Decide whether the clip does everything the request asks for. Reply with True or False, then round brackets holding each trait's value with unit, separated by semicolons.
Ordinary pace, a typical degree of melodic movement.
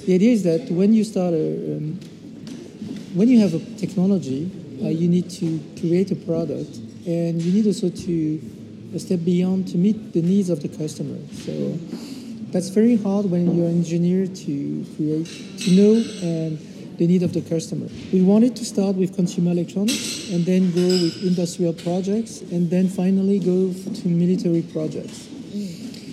True (170 wpm; 3.0 semitones)